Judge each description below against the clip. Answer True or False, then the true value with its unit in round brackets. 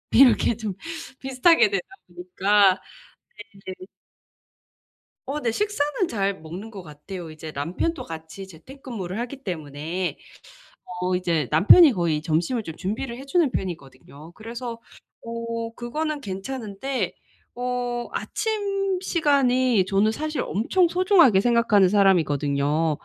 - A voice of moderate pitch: False (215 Hz)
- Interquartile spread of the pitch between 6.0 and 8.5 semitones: True (7.3 semitones)